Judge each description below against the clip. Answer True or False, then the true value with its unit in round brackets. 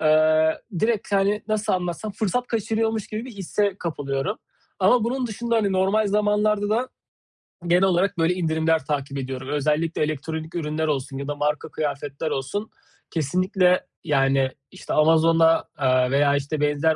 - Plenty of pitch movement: True (5.8 semitones)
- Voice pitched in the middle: True (165 Hz)